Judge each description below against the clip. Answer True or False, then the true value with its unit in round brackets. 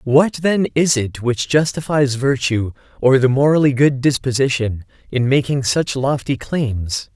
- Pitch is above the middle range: False (135 Hz)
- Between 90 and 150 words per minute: True (145 wpm)